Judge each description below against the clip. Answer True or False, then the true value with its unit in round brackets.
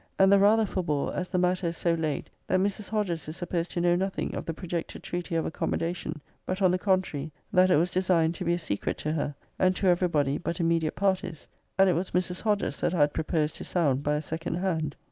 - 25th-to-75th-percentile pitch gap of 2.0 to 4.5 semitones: True (2.6 semitones)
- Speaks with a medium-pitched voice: True (175 Hz)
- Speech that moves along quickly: True (240 wpm)